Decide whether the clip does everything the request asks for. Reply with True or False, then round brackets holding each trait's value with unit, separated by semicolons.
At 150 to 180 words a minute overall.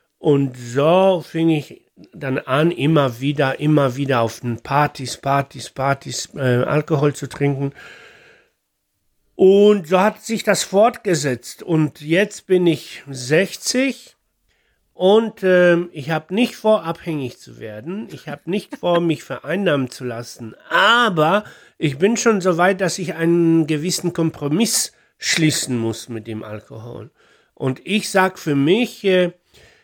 False (140 wpm)